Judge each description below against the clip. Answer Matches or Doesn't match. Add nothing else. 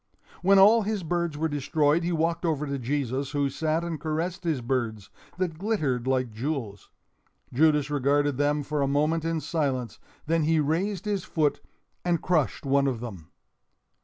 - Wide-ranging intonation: Doesn't match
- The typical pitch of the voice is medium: Matches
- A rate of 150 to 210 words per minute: Matches